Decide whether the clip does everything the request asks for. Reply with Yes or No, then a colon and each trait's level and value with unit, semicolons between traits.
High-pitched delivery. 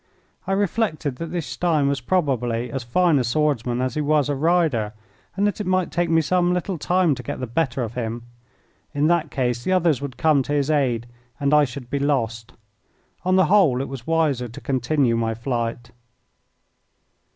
No: medium, 140 Hz